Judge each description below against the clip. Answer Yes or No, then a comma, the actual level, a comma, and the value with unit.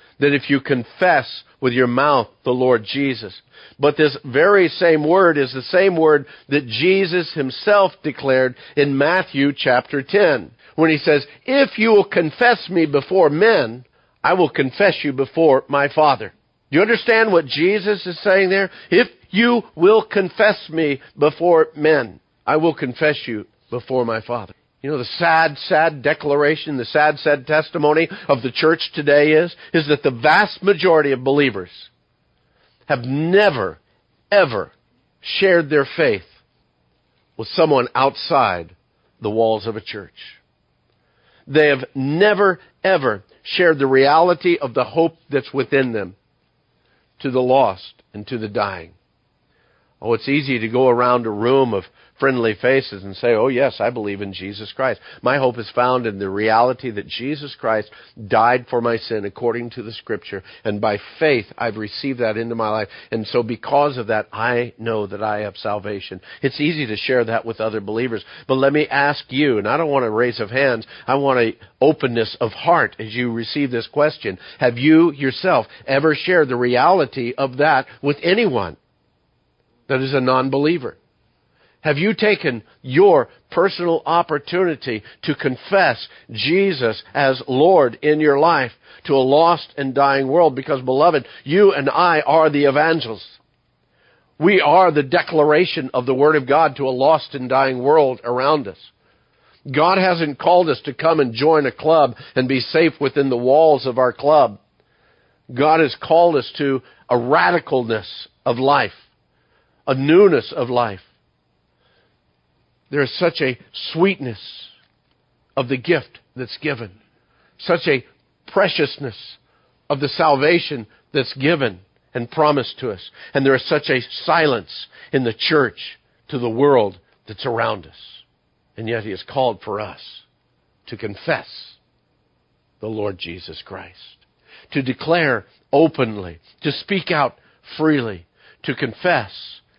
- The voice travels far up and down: No, average, 5.0 semitones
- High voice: No, medium, 140 Hz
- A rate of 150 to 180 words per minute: Yes, average, 155 wpm